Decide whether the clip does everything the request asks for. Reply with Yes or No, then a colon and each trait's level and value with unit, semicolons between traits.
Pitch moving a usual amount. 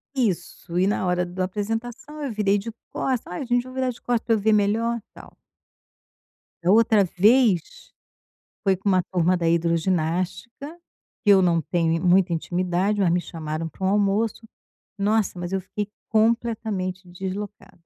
Yes: average, 3.9 semitones